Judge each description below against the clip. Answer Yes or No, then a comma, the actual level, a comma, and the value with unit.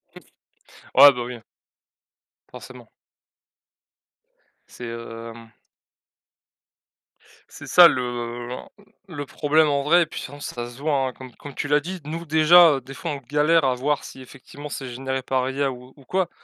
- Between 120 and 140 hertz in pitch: Yes, low, 135 Hz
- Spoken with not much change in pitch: No, average, 3.1 semitones